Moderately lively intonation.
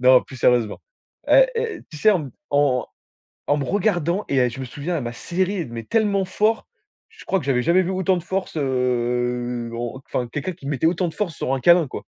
No: wide, 6.9 semitones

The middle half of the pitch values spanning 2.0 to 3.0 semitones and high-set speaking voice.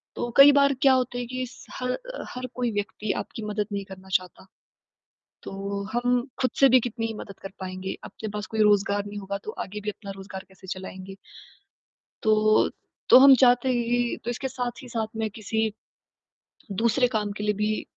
No: average, 3.5 semitones; high, 215 Hz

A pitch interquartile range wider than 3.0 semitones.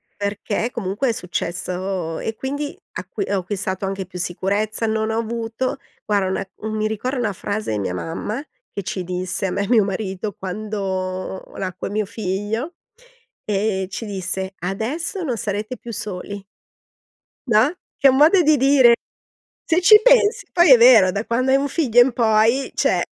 Yes: average, 4.4 semitones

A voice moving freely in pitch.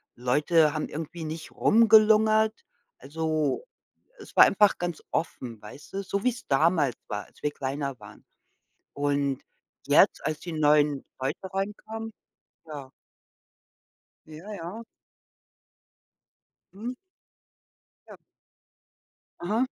Yes: wide, 6.3 semitones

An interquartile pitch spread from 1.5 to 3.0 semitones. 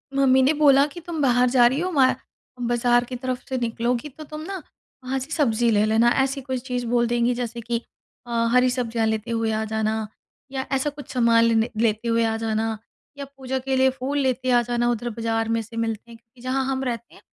Yes: narrow, 2.5 semitones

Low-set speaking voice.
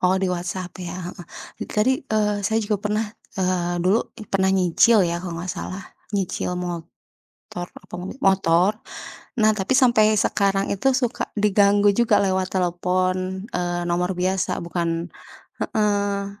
No: high, 190 Hz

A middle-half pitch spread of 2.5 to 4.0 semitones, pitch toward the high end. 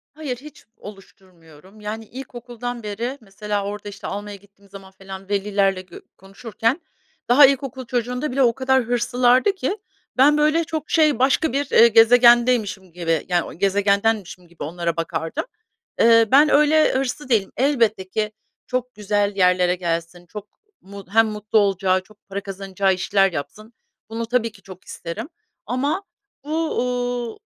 No: average, 4.5 semitones; high, 215 Hz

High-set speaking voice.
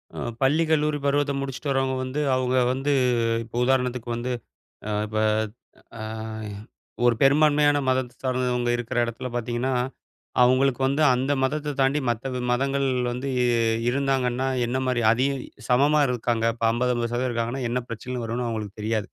No: low, 125 Hz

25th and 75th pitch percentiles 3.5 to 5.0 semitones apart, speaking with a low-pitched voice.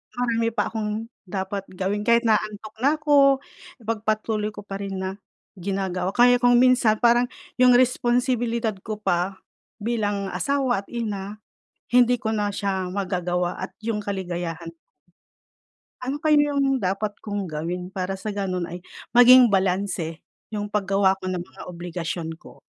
No: average, 4.1 semitones; high, 205 Hz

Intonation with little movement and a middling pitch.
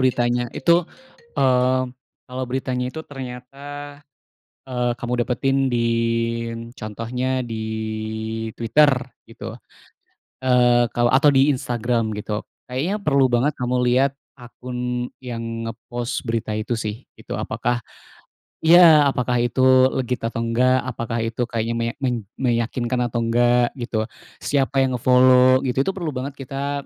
No: narrow, 2.1 semitones; low, 125 Hz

